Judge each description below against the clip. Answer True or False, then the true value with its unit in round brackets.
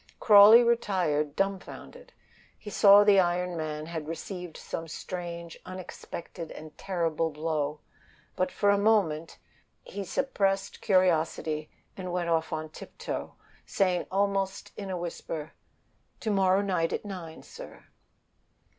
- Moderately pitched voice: True (180 Hz)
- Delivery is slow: True (130 wpm)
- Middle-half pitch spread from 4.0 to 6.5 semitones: False (3.5 semitones)